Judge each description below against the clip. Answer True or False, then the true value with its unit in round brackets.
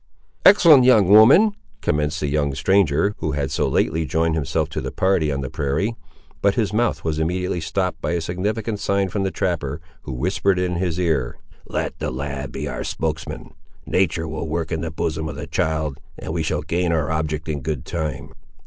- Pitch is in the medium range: False (80 Hz)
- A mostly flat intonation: False (3.8 semitones)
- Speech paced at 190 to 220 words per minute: True (195 wpm)